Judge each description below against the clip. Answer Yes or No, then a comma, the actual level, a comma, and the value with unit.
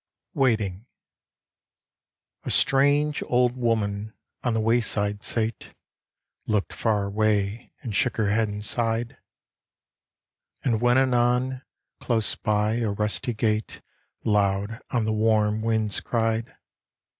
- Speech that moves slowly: Yes, slow, 110 wpm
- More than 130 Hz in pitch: No, low, 110 Hz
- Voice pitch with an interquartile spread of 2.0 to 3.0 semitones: Yes, narrow, 2.4 semitones